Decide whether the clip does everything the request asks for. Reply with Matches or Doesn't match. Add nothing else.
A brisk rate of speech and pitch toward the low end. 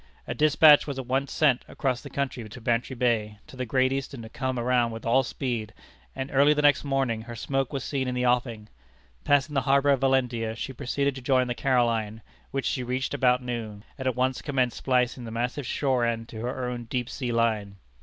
Matches